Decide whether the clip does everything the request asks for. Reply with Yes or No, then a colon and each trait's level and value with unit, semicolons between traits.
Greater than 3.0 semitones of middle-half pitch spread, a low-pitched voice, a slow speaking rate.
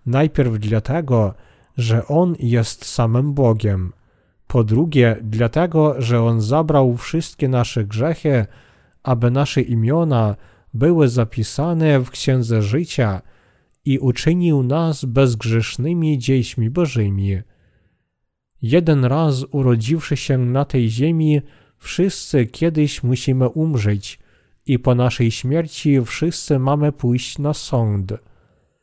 Yes: average, 4.5 semitones; low, 130 Hz; slow, 105 wpm